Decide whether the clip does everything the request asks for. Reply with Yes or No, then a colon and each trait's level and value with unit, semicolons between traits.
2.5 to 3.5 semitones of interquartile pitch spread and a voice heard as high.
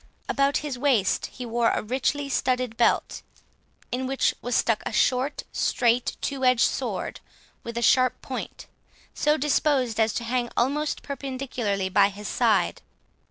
Yes: average, 2.8 semitones; very high, 250 Hz